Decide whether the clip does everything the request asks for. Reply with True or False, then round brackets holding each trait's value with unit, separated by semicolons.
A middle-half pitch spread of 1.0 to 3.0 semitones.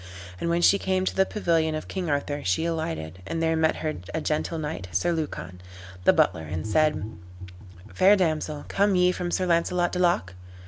False (3.5 semitones)